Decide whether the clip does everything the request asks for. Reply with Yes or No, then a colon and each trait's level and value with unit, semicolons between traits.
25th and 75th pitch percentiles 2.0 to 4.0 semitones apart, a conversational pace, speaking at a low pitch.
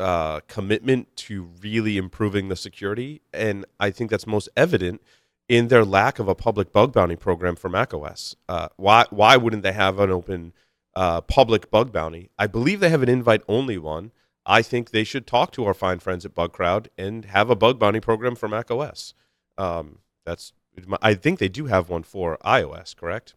Yes: average, 3.6 semitones; average, 190 wpm; low, 100 Hz